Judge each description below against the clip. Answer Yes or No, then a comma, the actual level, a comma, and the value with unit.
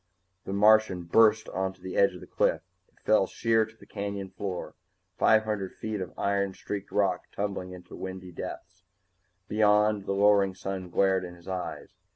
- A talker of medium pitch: No, low, 100 Hz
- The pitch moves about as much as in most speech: No, narrow, 2.1 semitones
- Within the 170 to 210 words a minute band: Yes, average, 175 wpm